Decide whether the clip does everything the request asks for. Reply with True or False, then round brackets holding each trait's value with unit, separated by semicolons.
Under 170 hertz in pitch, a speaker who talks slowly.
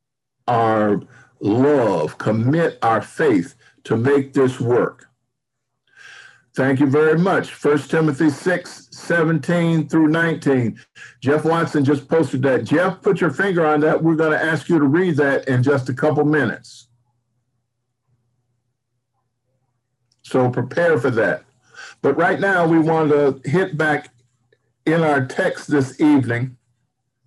True (140 Hz; 130 wpm)